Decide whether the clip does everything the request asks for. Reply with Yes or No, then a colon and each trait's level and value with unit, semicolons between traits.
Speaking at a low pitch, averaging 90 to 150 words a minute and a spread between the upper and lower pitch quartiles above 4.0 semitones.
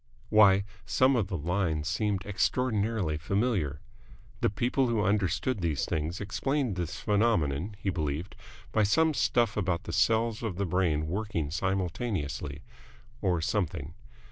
Yes: low, 100 Hz; slow, 135 wpm; average, 4.8 semitones